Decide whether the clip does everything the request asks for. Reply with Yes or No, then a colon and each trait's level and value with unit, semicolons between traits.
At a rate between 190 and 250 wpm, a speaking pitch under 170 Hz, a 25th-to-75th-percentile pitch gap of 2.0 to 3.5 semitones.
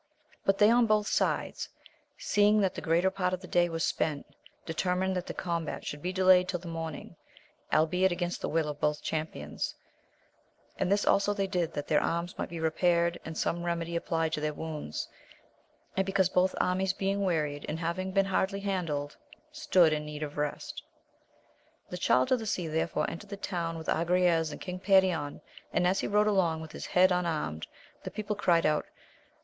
No: average, 195 wpm; medium, 175 Hz; average, 2.9 semitones